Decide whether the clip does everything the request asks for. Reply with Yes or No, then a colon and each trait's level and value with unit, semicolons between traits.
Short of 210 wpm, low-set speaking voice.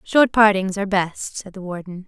No: average, 200 wpm; high, 195 Hz